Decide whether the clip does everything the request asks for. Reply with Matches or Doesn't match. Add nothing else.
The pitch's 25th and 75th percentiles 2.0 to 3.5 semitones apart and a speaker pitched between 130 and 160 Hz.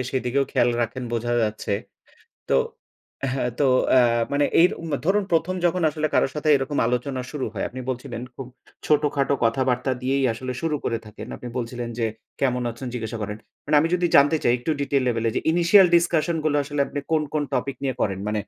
Doesn't match